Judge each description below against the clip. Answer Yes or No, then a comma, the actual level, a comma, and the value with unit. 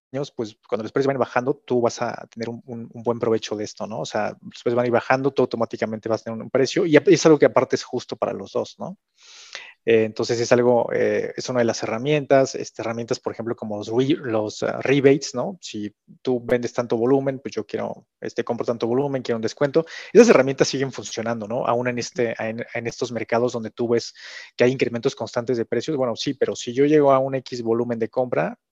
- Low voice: Yes, low, 120 Hz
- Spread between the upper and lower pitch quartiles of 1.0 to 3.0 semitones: Yes, narrow, 2.5 semitones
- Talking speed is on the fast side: Yes, fast, 230 wpm